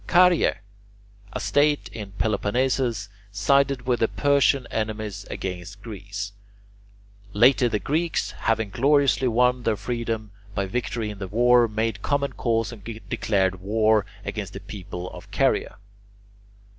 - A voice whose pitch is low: Yes, low, 115 Hz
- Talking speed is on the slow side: Yes, slow, 130 wpm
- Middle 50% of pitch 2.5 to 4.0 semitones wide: Yes, average, 3.7 semitones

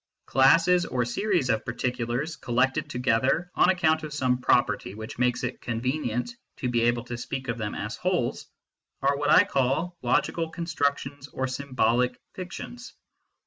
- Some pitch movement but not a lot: Yes, average, 4.7 semitones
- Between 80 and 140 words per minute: No, average, 160 wpm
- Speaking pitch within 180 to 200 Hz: No, low, 130 Hz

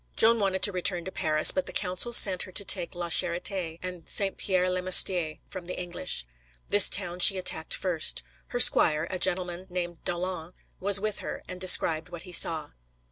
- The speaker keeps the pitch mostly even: Yes, narrow, 1.6 semitones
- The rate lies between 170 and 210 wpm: Yes, average, 190 wpm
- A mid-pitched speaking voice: Yes, medium, 180 Hz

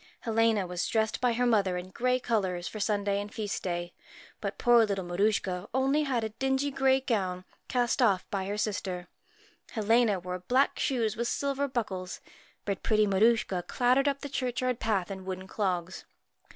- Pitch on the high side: Yes, high, 215 Hz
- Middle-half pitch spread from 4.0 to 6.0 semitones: Yes, average, 4.6 semitones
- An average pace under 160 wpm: No, average, 180 wpm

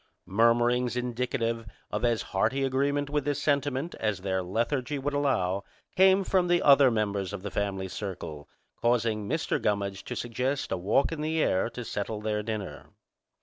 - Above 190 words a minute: No, average, 165 wpm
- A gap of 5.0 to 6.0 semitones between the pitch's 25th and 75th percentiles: Yes, wide, 5.5 semitones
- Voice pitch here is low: Yes, low, 120 Hz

